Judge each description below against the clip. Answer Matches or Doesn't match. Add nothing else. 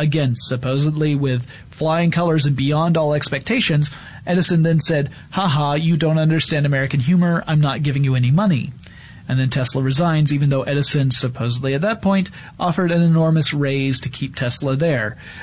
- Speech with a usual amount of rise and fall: Matches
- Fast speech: Doesn't match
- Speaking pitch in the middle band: Matches